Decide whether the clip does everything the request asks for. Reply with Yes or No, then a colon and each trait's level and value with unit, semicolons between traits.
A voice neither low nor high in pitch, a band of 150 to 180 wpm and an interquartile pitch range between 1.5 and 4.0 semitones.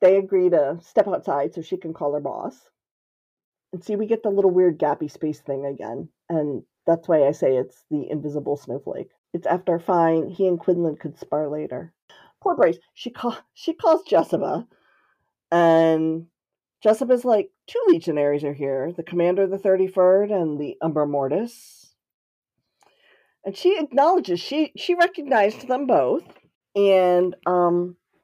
No: medium, 180 Hz; average, 155 wpm; average, 4.9 semitones